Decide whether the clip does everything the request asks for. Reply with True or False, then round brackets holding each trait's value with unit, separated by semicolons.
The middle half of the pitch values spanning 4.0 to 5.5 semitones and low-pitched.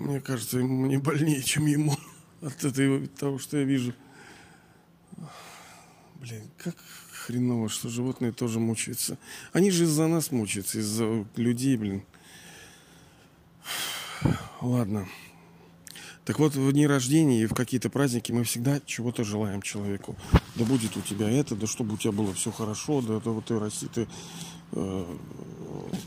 True (4.4 semitones; 125 Hz)